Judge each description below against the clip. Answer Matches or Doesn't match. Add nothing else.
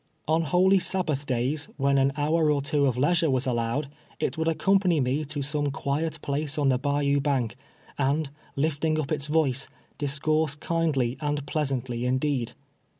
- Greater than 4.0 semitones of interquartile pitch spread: Doesn't match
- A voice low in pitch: Doesn't match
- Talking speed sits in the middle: Matches